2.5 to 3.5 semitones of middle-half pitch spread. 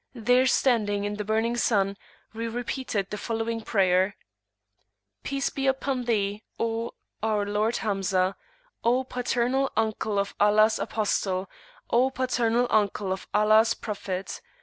Yes: average, 2.9 semitones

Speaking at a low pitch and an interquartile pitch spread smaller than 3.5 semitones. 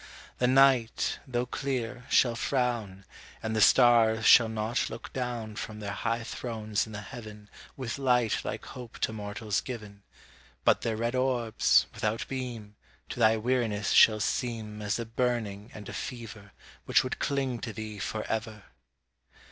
Yes: low, 115 Hz; narrow, 2.5 semitones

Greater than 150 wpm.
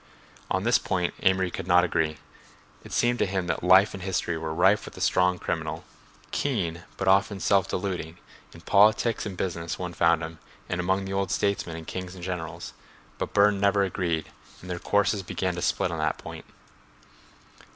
Yes: average, 185 wpm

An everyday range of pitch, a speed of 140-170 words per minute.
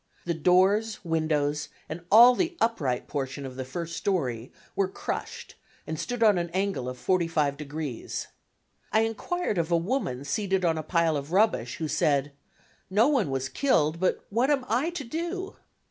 No: wide, 7.3 semitones; average, 165 wpm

